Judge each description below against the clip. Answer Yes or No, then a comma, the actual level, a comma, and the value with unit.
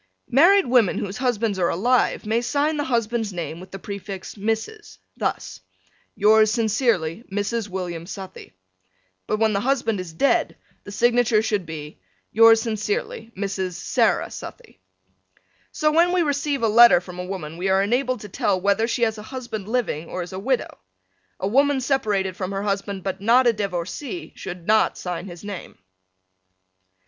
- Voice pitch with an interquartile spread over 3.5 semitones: Yes, average, 4.2 semitones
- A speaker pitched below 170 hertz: No, high, 215 Hz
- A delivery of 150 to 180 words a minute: Yes, average, 165 wpm